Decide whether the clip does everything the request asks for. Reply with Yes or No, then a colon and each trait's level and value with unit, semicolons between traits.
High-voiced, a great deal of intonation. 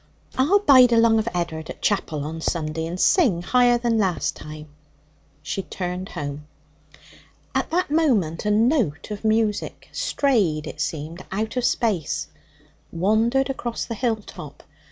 Yes: high, 210 Hz; wide, 6.8 semitones